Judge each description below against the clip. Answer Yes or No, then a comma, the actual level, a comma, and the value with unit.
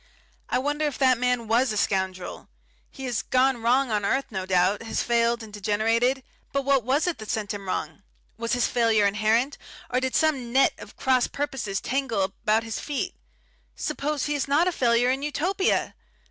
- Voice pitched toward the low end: No, high, 240 Hz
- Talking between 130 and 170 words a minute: No, average, 185 wpm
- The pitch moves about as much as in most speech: Yes, average, 3.9 semitones